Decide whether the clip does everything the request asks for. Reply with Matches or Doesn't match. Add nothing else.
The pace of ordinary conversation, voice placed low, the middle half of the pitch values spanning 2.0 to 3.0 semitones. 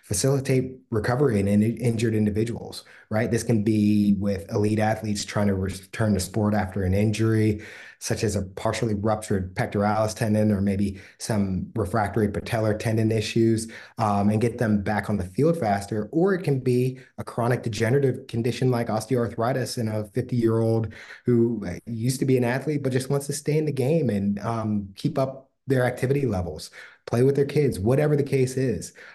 Doesn't match